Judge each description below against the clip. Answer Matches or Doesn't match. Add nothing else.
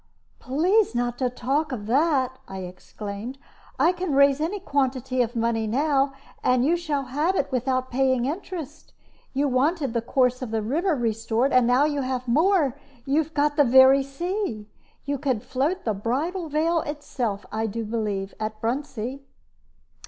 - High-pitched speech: Matches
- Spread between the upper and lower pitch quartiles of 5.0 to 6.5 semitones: Doesn't match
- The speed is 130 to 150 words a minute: Doesn't match